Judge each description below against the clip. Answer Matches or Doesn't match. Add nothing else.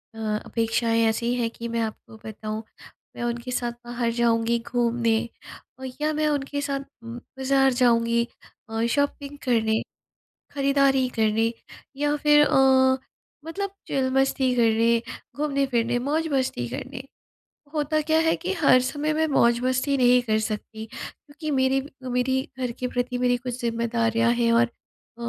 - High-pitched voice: Matches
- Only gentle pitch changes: Doesn't match